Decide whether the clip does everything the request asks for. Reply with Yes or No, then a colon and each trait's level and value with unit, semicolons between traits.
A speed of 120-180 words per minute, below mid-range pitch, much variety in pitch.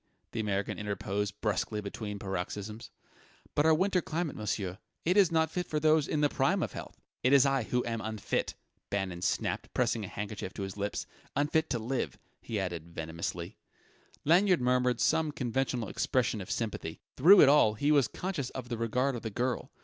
No: average, 190 wpm; low, 120 Hz; wide, 6.1 semitones